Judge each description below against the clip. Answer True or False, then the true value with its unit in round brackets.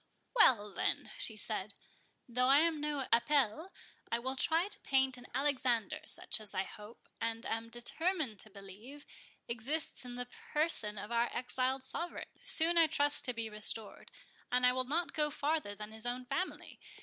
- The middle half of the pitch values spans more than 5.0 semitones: False (4.7 semitones)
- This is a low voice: False (250 Hz)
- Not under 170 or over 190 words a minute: True (175 wpm)